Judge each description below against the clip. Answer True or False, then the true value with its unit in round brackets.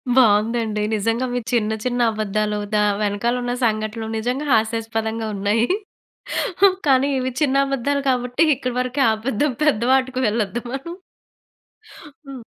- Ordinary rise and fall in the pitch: True (3.1 semitones)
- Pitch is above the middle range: True (235 Hz)